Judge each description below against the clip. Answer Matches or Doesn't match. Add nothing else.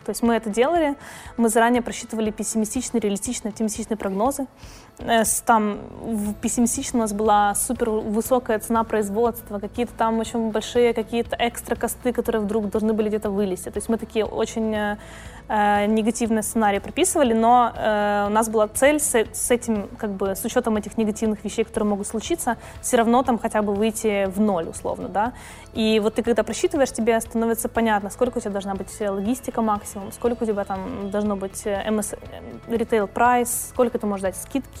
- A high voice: Matches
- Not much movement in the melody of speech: Matches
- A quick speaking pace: Matches